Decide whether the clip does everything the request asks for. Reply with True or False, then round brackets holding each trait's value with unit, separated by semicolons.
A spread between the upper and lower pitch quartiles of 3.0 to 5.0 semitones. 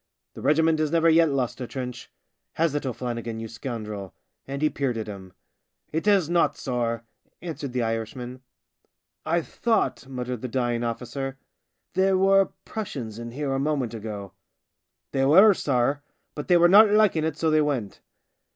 False (5.4 semitones)